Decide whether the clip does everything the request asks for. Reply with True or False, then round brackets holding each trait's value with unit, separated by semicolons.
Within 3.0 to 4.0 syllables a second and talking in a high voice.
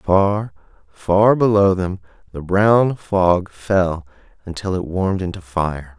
False (3.8 syllables/s; 95 Hz)